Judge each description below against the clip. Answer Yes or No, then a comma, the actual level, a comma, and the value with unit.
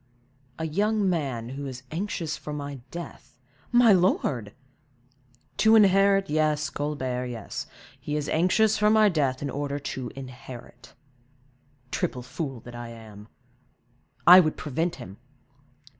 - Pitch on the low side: No, medium, 150 Hz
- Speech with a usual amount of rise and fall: No, wide, 6.2 semitones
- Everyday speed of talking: No, slow, 130 wpm